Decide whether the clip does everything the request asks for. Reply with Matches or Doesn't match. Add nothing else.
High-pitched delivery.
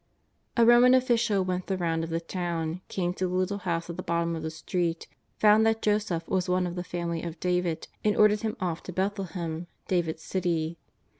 Doesn't match